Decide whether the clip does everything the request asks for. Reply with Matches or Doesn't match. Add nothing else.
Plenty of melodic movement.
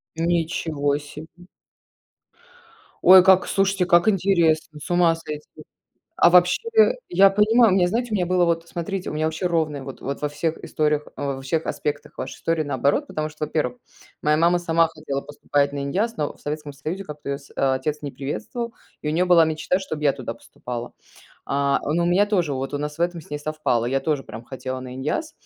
Doesn't match